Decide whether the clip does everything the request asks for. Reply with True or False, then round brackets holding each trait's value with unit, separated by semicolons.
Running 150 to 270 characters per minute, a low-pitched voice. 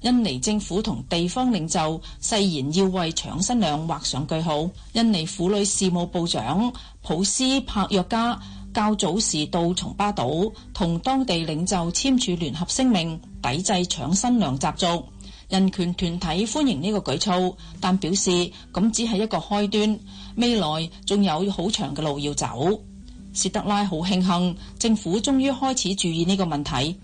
False (235 characters per minute; 190 Hz)